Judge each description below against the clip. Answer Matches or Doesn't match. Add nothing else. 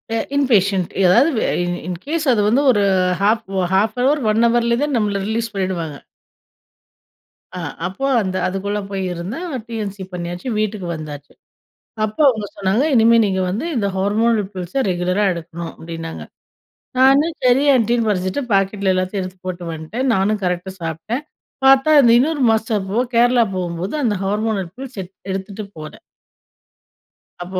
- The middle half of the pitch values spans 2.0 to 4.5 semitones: Matches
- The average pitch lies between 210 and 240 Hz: Doesn't match